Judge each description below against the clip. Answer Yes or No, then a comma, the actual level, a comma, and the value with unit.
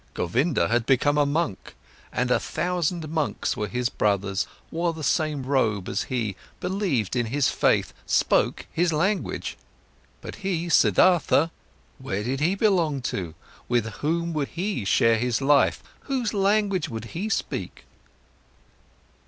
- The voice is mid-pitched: Yes, medium, 145 Hz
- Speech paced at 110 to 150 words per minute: Yes, average, 140 wpm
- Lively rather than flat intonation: Yes, wide, 6.6 semitones